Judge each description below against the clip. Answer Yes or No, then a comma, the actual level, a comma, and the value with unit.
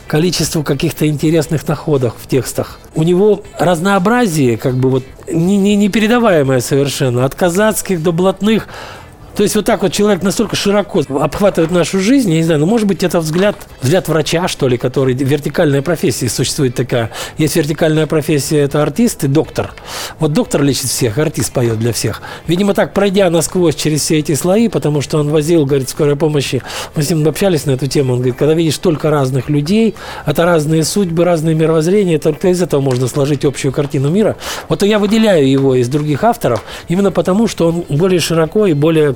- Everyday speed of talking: No, fast, 185 wpm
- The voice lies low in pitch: No, medium, 160 Hz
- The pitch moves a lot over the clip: No, average, 4.6 semitones